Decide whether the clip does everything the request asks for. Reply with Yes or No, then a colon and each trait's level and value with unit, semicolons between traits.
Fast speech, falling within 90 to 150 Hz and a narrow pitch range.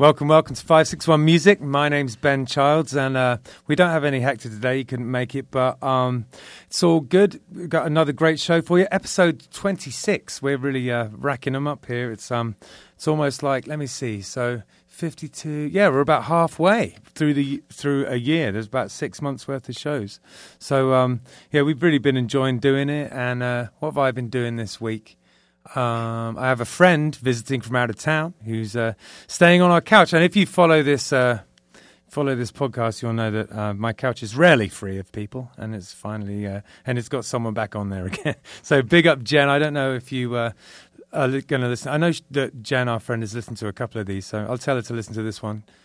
No: fast, 235 wpm; low, 135 Hz; average, 4.5 semitones